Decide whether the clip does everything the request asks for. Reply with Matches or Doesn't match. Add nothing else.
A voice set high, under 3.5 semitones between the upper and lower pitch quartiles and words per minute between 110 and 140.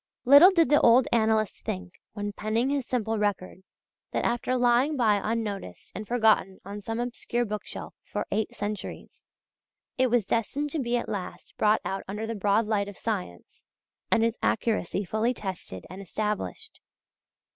Doesn't match